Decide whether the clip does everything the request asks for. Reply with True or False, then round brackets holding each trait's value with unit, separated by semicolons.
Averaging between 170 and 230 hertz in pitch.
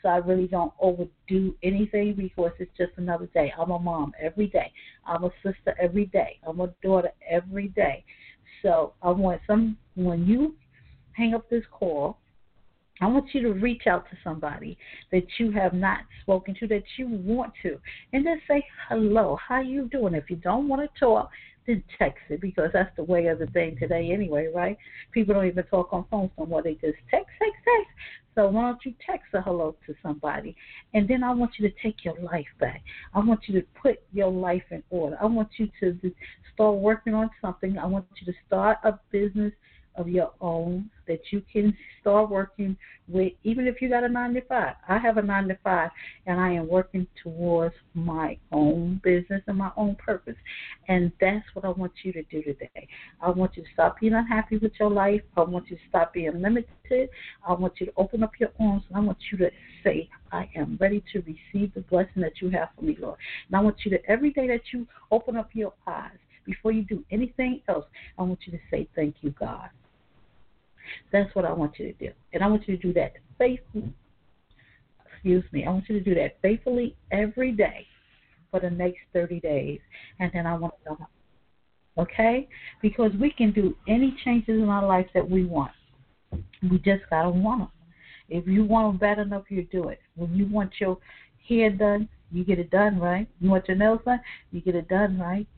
True (190 Hz)